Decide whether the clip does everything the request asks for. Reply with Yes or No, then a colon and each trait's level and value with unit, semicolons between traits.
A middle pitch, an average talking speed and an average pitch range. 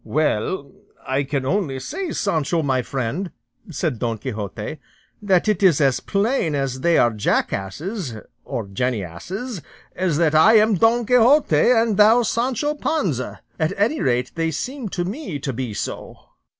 No: medium, 165 Hz; average, 150 wpm; wide, 8.8 semitones